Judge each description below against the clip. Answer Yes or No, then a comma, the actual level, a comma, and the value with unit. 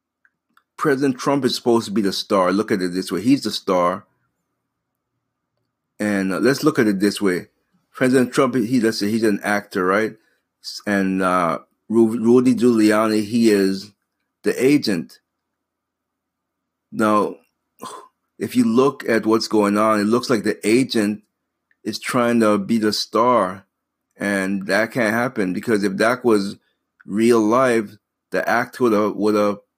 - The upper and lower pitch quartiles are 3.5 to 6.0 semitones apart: No, average, 2.7 semitones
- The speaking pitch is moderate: No, low, 110 Hz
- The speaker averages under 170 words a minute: Yes, average, 150 wpm